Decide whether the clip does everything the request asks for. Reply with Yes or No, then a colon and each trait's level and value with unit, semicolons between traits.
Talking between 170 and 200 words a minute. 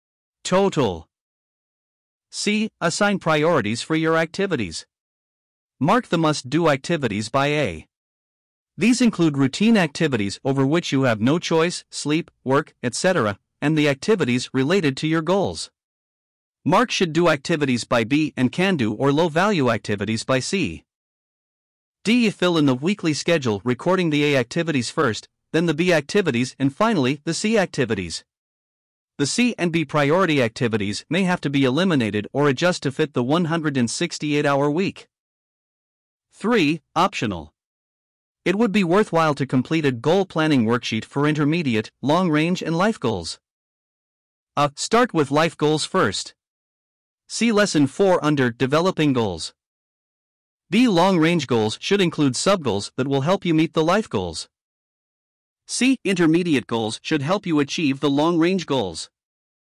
No: average, 140 wpm